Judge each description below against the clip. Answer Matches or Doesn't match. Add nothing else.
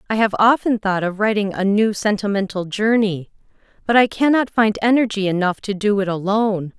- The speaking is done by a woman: Matches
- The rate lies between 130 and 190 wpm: Matches